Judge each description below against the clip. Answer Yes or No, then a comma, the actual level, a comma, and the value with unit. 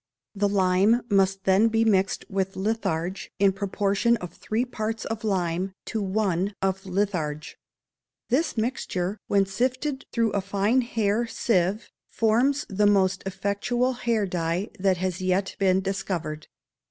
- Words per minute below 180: Yes, average, 140 wpm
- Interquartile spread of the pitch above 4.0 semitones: No, average, 2.9 semitones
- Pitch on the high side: Yes, high, 200 Hz